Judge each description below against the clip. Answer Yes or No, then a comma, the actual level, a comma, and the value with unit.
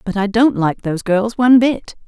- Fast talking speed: Yes, fast, 230 wpm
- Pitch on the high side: Yes, high, 215 Hz